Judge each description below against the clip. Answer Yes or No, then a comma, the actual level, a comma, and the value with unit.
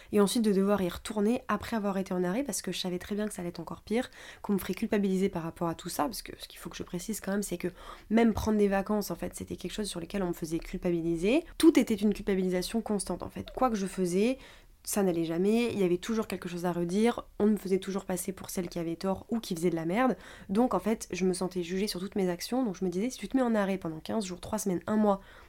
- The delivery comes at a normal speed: No, fast, 295 wpm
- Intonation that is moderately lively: Yes, average, 3.0 semitones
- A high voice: Yes, high, 195 Hz